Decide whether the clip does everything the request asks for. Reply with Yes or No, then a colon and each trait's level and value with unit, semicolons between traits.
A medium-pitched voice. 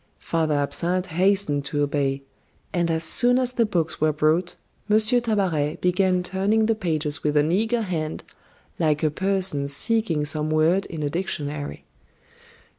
Yes: medium, 170 Hz